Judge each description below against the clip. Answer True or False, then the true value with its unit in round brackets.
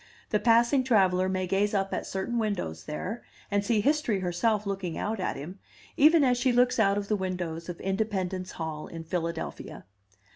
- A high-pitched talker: True (195 Hz)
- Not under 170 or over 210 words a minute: True (180 wpm)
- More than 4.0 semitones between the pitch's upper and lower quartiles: False (3.6 semitones)